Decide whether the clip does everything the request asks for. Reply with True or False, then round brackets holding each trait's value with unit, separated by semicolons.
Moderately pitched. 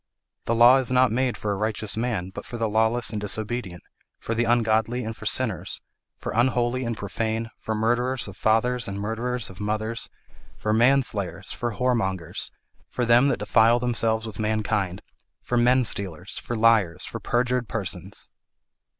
False (115 Hz)